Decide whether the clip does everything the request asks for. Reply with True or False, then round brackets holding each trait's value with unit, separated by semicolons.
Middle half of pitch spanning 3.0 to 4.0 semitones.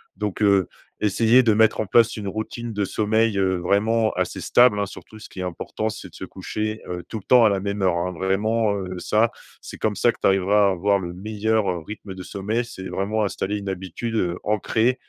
False (2.5 semitones)